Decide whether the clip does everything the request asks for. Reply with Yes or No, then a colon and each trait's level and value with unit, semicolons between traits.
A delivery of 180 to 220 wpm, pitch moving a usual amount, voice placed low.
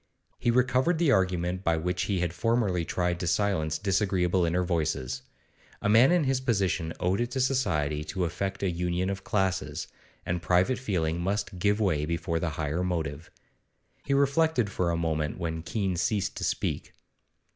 No: average, 170 wpm; average, 3.8 semitones; very low, 90 Hz